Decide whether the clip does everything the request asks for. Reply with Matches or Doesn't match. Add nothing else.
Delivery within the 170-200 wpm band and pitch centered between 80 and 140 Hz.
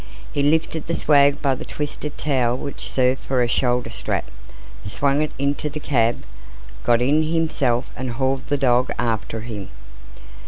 Doesn't match